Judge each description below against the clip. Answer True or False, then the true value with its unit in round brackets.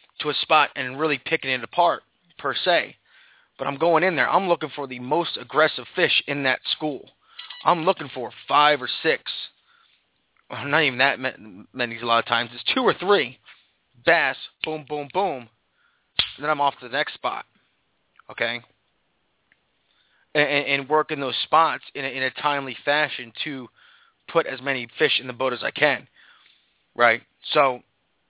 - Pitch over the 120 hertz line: True (140 Hz)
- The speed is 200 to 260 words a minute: False (175 wpm)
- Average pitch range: True (3.4 semitones)